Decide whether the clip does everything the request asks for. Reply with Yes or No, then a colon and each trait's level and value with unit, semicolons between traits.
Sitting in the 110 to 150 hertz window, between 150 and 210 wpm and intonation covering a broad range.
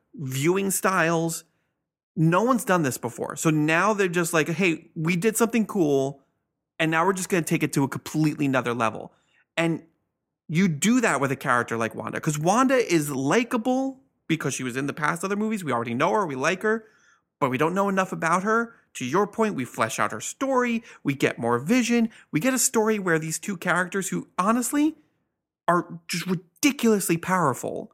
No: medium, 170 Hz; average, 195 wpm; wide, 6.3 semitones